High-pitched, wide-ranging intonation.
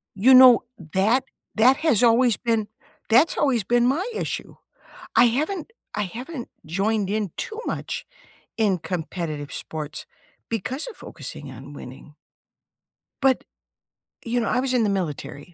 Yes: high, 225 Hz; wide, 6.0 semitones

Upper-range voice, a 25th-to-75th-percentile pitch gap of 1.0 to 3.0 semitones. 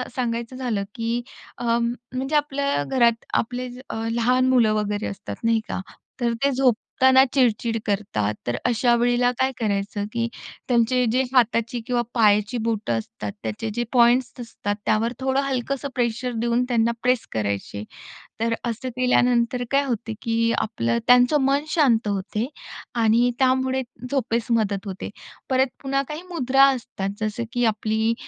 Yes: high, 235 Hz; narrow, 2.6 semitones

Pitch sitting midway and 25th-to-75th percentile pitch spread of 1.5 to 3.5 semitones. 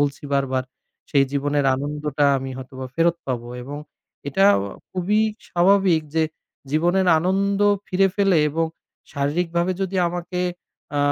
No: medium, 165 Hz; average, 4.6 semitones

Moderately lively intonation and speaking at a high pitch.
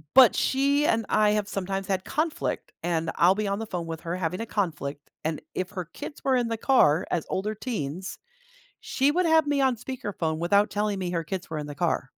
No: wide, 6.0 semitones; high, 195 Hz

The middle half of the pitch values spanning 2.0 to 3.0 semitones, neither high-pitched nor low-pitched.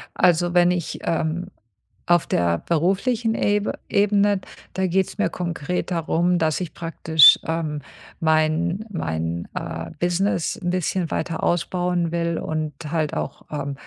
Yes: narrow, 2.4 semitones; medium, 170 Hz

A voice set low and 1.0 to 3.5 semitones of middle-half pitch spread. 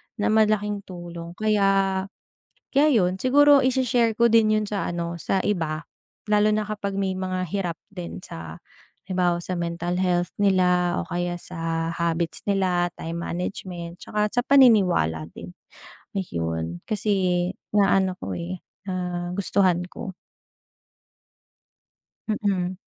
No: medium, 185 Hz; average, 3.2 semitones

